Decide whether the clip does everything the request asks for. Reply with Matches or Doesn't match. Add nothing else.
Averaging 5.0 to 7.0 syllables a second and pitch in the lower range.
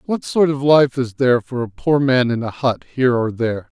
Matches